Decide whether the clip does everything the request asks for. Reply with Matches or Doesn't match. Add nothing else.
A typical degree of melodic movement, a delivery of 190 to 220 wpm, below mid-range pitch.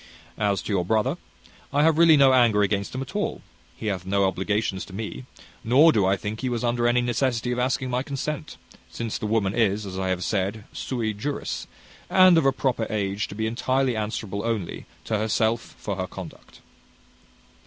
Matches